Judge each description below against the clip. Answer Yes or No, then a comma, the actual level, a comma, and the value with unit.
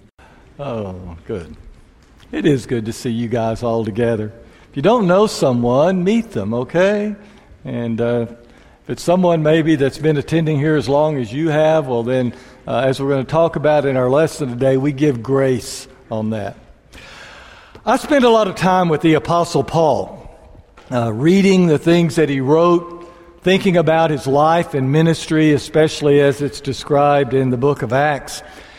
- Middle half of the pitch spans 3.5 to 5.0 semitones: Yes, average, 4.3 semitones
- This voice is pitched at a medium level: Yes, medium, 145 Hz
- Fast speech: No, average, 175 wpm